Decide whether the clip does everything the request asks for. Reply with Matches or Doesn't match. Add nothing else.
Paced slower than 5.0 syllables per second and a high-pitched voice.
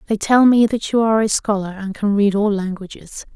Doesn't match